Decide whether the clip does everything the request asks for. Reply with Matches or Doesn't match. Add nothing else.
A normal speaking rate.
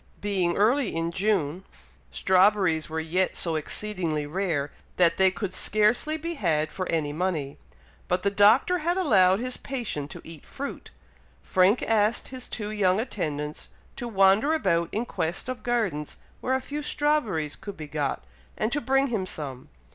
Matches